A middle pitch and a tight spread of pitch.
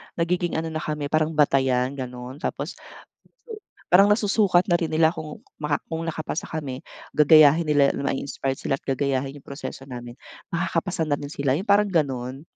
No: medium, 150 Hz; average, 3.4 semitones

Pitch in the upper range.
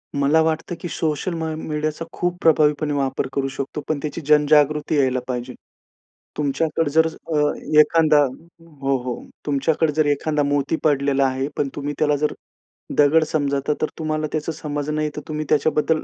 No: medium, 150 Hz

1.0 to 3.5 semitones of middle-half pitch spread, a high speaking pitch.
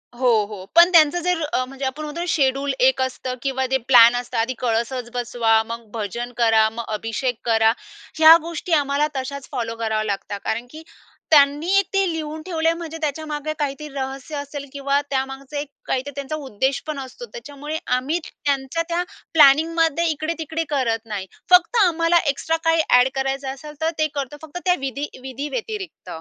No: average, 3.9 semitones; very high, 280 Hz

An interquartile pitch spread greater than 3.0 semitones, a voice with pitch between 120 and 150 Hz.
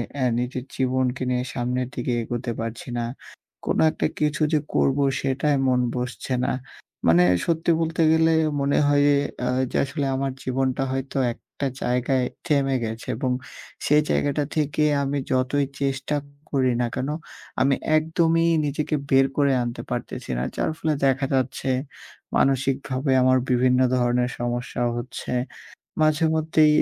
No: narrow, 2.4 semitones; low, 135 Hz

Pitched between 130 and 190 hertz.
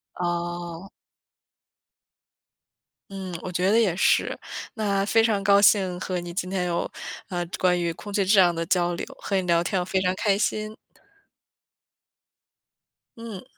Yes: medium, 185 Hz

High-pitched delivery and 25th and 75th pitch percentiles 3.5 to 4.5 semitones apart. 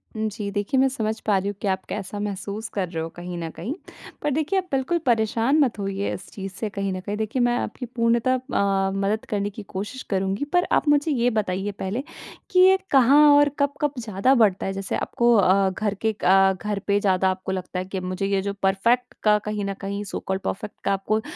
Yes: high, 205 Hz; average, 3.8 semitones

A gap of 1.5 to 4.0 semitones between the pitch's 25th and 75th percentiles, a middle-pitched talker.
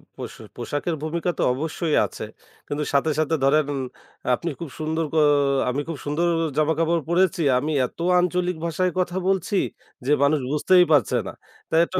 Yes: average, 2.8 semitones; medium, 160 Hz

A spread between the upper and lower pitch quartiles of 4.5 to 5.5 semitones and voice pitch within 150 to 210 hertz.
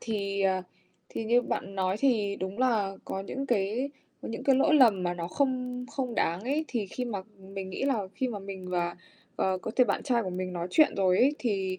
Yes: average, 4.9 semitones; high, 205 Hz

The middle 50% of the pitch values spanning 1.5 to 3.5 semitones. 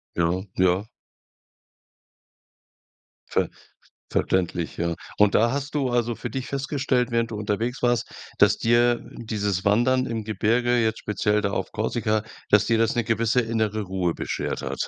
Yes: average, 2.8 semitones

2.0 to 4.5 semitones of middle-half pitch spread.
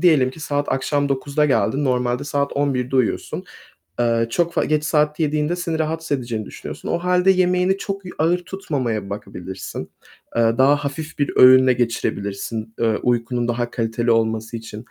No: average, 4.9 semitones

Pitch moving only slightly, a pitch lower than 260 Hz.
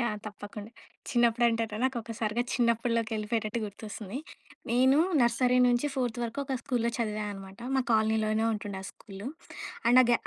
Yes: narrow, 2.2 semitones; high, 230 Hz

